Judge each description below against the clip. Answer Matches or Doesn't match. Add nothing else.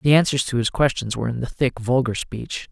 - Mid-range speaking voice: Doesn't match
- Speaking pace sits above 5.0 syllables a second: Matches